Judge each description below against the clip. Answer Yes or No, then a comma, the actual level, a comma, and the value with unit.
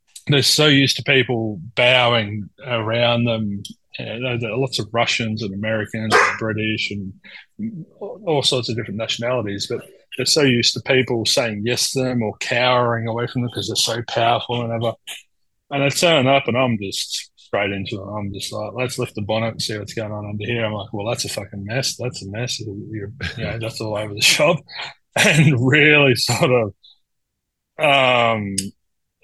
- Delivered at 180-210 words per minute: Yes, average, 190 wpm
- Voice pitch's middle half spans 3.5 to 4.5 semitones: No, average, 2.9 semitones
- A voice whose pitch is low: Yes, low, 115 Hz